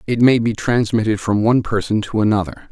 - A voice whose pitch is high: No, low, 110 Hz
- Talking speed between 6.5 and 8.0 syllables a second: No, 5.8 syllables/s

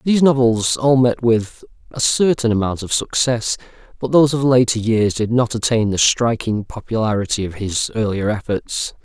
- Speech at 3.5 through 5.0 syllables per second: Yes, 4.8 syllables/s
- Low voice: Yes, low, 115 Hz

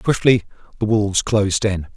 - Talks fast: No, average, 155 wpm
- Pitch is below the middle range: Yes, low, 105 Hz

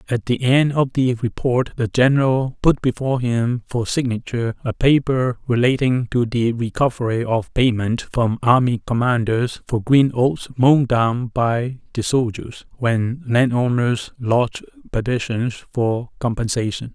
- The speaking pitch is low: Yes, low, 120 Hz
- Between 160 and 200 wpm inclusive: No, slow, 135 wpm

